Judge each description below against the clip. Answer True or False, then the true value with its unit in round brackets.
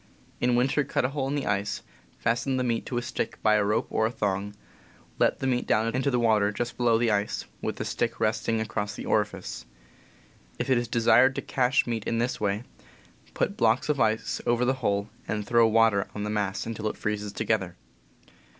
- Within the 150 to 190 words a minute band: False (205 wpm)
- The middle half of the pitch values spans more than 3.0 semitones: False (2.6 semitones)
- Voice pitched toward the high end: False (115 Hz)